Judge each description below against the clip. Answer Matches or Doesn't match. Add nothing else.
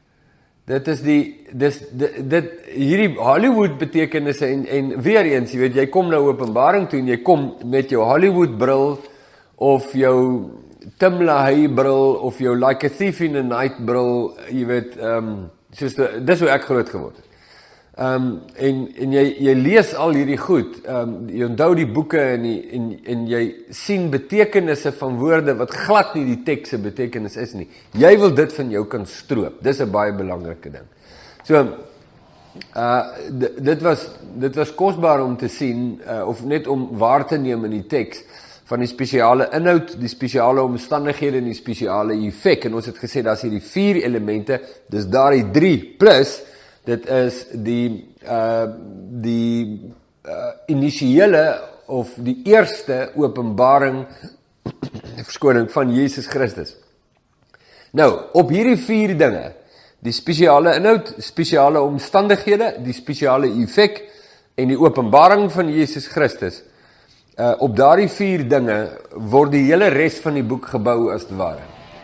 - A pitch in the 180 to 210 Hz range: Doesn't match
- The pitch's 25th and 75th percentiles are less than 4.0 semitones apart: Doesn't match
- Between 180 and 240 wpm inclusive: Doesn't match